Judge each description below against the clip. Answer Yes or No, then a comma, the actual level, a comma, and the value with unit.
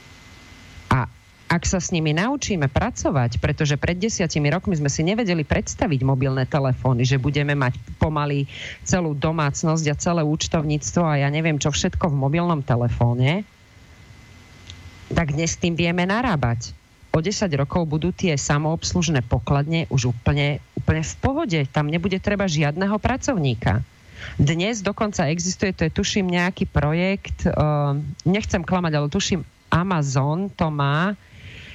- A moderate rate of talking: Yes, average, 135 wpm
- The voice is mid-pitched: Yes, medium, 150 Hz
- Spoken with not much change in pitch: No, average, 5.3 semitones